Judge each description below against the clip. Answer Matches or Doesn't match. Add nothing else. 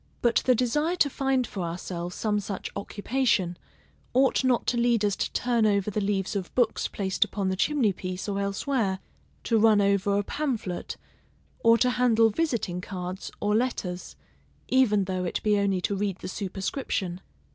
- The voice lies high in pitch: Matches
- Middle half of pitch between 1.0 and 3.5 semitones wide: Doesn't match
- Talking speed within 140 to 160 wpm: Doesn't match